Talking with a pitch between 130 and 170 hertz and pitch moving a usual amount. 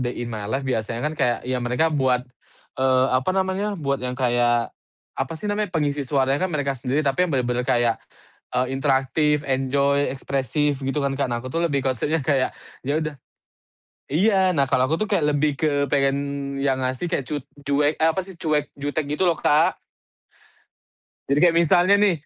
Yes: medium, 140 Hz; average, 3.3 semitones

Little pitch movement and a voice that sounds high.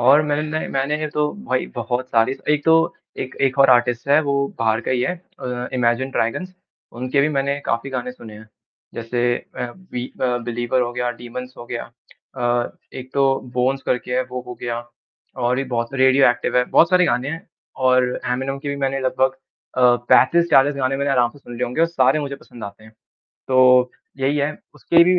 No: narrow, 2.3 semitones; low, 130 Hz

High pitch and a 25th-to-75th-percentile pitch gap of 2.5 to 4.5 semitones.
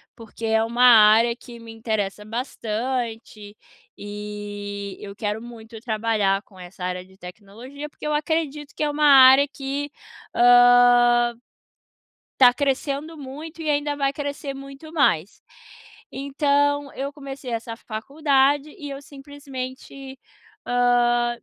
Yes: high, 245 Hz; average, 4.2 semitones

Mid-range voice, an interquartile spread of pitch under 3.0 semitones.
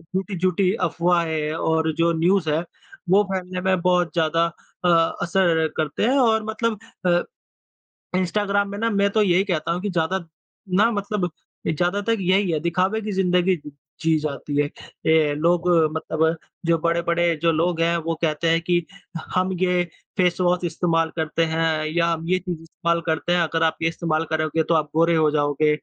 Yes: medium, 170 Hz; narrow, 2.5 semitones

